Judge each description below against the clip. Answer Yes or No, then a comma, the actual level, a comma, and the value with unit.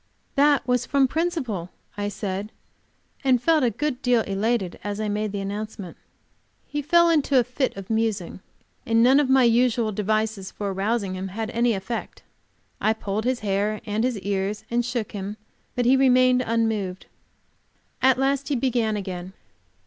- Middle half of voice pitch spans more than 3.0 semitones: Yes, average, 3.8 semitones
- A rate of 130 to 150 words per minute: No, average, 165 wpm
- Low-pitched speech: No, high, 225 Hz